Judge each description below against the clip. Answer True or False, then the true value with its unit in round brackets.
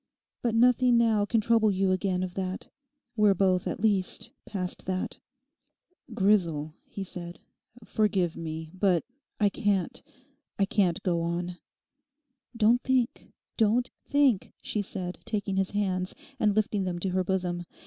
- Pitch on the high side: True (195 Hz)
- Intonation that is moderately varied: True (3.0 semitones)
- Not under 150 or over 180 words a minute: False (140 wpm)